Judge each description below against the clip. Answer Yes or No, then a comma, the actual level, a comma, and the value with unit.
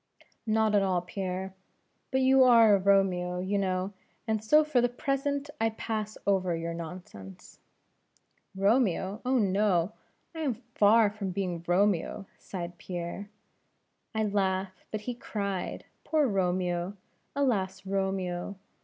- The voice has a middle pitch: No, high, 195 Hz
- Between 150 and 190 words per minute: No, slow, 135 wpm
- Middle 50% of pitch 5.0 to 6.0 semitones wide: No, average, 3.2 semitones